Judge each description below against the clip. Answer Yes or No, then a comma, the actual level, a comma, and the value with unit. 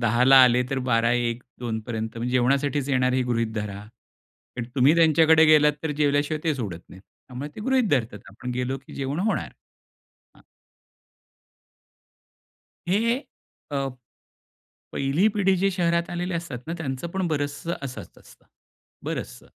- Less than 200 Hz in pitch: Yes, low, 135 Hz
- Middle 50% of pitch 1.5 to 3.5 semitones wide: No, average, 5.0 semitones